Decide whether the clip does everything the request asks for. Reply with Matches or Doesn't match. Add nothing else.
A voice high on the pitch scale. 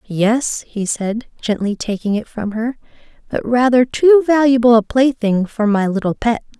Matches